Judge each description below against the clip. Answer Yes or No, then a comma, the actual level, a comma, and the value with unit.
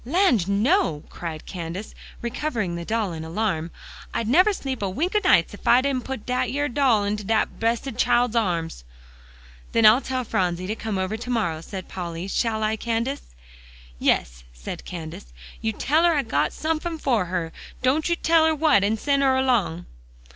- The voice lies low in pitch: No, high, 225 Hz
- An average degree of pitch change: No, wide, 6.6 semitones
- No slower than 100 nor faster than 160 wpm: No, average, 185 wpm